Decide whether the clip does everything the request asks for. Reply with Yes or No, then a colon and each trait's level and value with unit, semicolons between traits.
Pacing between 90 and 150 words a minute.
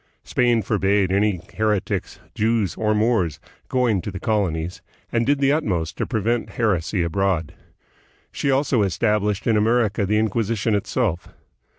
Yes: average, 145 wpm